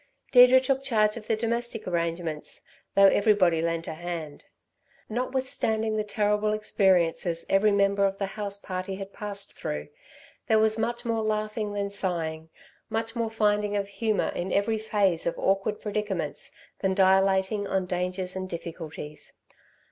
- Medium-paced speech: Yes, average, 150 wpm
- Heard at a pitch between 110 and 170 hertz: No, high, 200 Hz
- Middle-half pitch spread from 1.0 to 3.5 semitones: Yes, average, 3.0 semitones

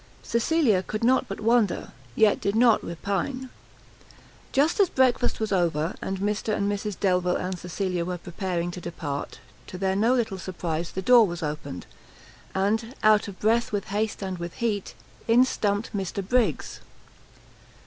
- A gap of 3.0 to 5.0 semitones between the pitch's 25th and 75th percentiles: Yes, average, 3.9 semitones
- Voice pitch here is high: Yes, high, 200 Hz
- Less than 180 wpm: Yes, average, 160 wpm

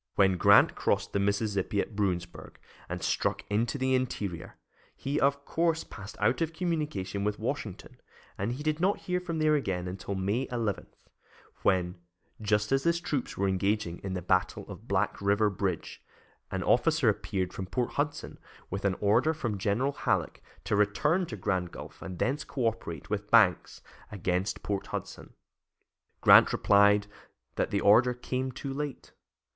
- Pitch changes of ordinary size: No, wide, 5.9 semitones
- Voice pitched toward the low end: Yes, low, 105 Hz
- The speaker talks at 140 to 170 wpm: Yes, average, 160 wpm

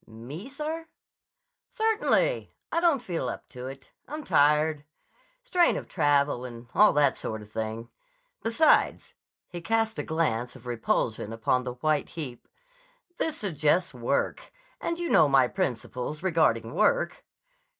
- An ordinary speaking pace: No, slow, 130 wpm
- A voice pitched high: No, medium, 150 Hz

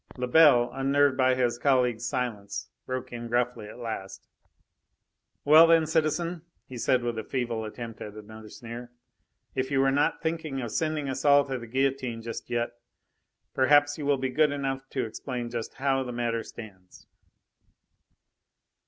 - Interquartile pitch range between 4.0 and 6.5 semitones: No, average, 3.0 semitones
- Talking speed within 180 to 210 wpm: No, average, 160 wpm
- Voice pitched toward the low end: Yes, low, 130 Hz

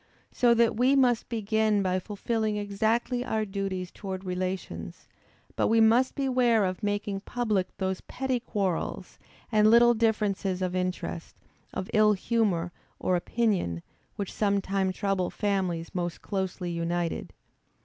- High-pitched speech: Yes, high, 205 Hz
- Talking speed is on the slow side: Yes, slow, 130 wpm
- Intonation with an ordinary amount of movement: Yes, average, 3.4 semitones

